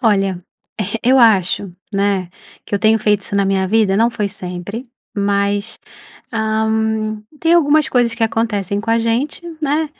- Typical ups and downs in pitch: No, narrow, 2.3 semitones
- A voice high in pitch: Yes, high, 215 Hz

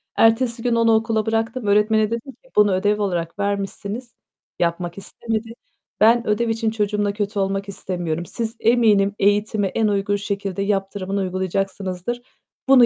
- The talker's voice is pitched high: Yes, high, 205 Hz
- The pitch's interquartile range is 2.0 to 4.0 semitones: Yes, narrow, 2.4 semitones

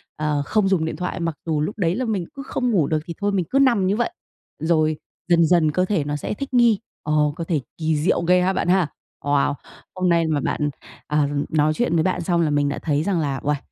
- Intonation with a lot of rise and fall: No, average, 3.9 semitones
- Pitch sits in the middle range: Yes, medium, 170 Hz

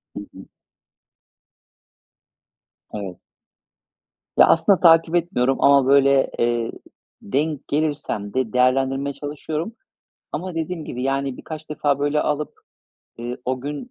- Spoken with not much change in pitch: No, average, 3.2 semitones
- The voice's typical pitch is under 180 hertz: Yes, medium, 140 Hz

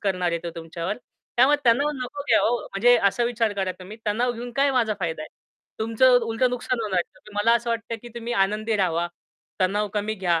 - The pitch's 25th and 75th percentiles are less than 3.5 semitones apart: No, average, 4.1 semitones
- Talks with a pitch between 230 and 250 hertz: No, high, 220 Hz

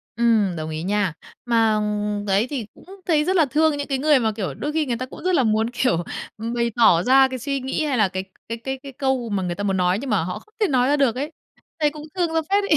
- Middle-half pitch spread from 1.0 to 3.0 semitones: No, wide, 5.5 semitones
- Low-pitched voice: No, high, 245 Hz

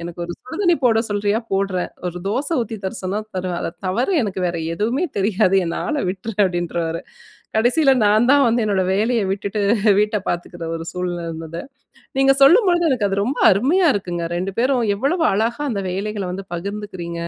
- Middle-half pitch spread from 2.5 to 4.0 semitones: No, average, 5.0 semitones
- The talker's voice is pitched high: Yes, high, 205 Hz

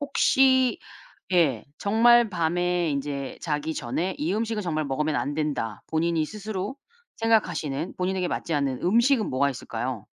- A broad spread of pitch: Yes, wide, 6.6 semitones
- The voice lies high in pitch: No, medium, 170 Hz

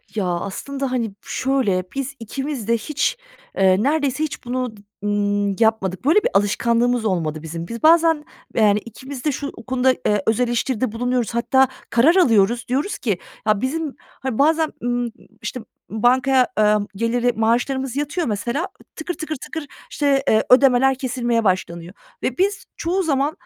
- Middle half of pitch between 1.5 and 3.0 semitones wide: No, average, 4.3 semitones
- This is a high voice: Yes, high, 245 Hz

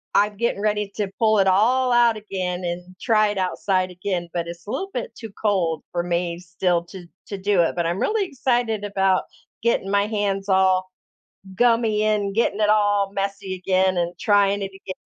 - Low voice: No, high, 200 Hz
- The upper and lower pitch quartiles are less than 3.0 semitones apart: Yes, narrow, 2.5 semitones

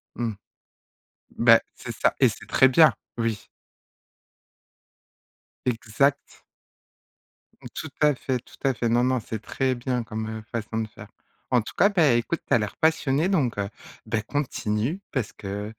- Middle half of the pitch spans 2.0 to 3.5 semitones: No, average, 3.9 semitones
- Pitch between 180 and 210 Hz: No, low, 120 Hz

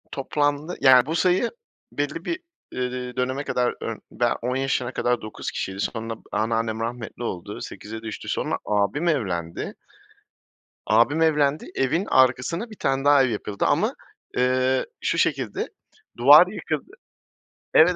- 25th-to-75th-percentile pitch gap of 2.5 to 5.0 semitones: Yes, average, 4.3 semitones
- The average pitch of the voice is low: Yes, low, 130 Hz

